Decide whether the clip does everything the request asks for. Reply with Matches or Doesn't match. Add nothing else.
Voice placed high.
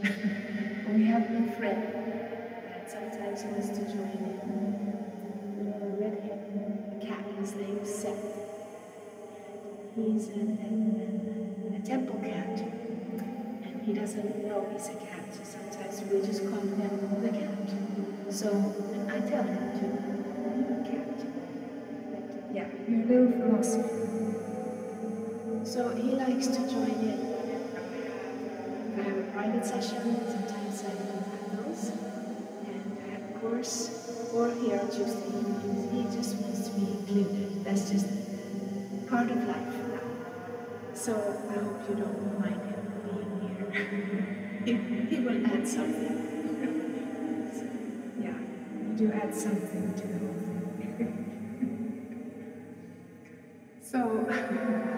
Matches